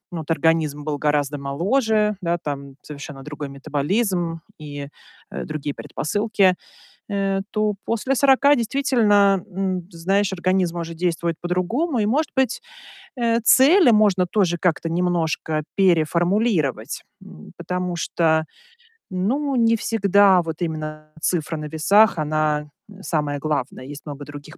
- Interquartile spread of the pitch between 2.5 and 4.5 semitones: No, average, 5.3 semitones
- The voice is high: No, medium, 175 Hz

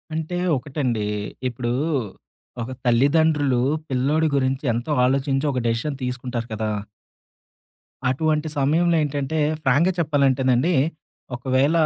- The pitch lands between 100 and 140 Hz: Yes, low, 135 Hz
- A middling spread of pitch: Yes, average, 3.4 semitones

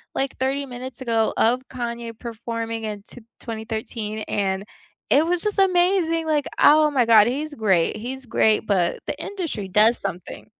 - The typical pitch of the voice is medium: No, high, 235 Hz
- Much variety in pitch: No, average, 4.8 semitones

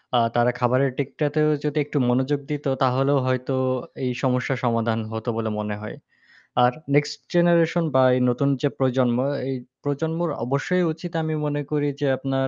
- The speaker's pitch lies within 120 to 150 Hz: Yes, low, 135 Hz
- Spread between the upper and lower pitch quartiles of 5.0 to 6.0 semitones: No, average, 2.9 semitones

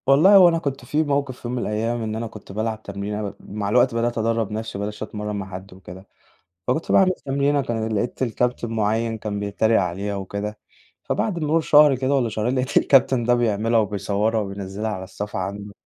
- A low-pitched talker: Yes, low, 110 Hz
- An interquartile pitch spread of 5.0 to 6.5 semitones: No, average, 3.7 semitones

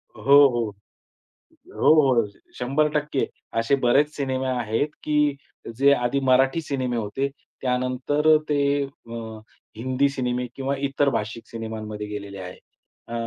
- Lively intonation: No, average, 3.5 semitones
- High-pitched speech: No, low, 130 Hz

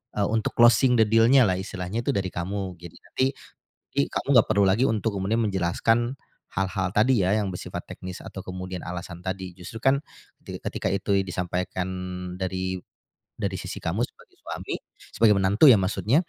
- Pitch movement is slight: No, average, 3.4 semitones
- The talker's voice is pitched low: Yes, very low, 95 Hz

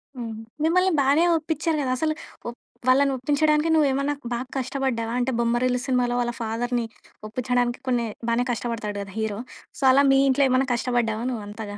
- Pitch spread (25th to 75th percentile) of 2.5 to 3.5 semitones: Yes, average, 2.9 semitones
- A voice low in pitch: No, very high, 250 Hz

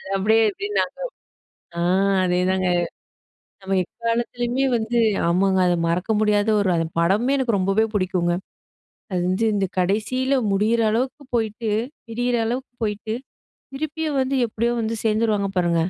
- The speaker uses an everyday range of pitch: Yes, average, 3.9 semitones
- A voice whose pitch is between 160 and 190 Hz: No, high, 220 Hz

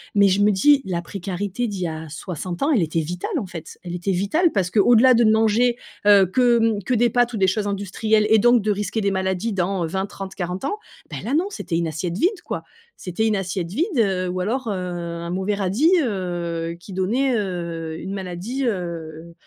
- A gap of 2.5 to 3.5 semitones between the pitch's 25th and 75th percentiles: No, average, 4.1 semitones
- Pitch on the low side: No, high, 195 Hz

